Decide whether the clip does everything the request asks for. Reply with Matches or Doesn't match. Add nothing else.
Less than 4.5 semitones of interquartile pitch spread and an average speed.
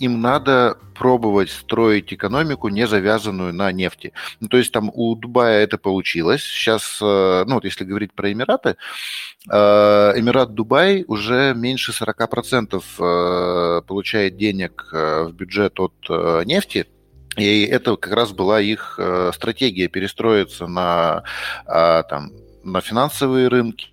Matches